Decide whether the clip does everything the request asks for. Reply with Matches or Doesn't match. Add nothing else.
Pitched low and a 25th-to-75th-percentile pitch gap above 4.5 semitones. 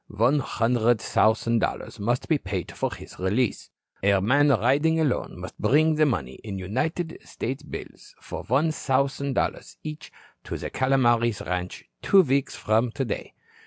Matches